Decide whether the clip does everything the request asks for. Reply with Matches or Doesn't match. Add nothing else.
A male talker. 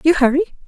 Doesn't match